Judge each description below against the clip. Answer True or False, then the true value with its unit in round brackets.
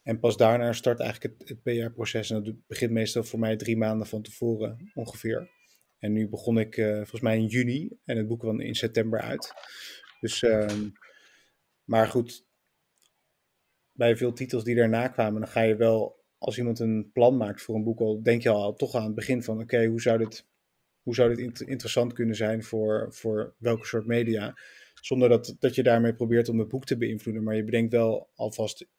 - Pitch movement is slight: True (1.4 semitones)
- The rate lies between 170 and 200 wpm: True (195 wpm)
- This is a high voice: False (115 Hz)